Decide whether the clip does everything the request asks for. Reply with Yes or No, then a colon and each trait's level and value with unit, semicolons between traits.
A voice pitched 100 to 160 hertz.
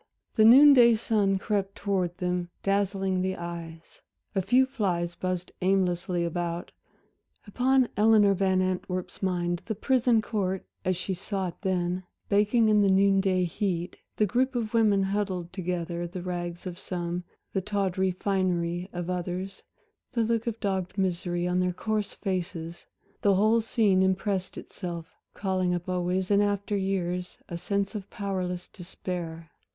No: high, 190 Hz